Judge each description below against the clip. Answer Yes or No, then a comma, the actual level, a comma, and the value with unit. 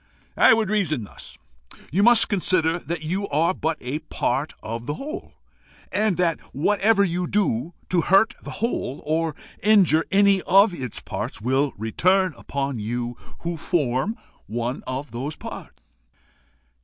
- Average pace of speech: Yes, average, 145 wpm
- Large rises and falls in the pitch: Yes, wide, 6.6 semitones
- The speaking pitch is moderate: Yes, medium, 165 Hz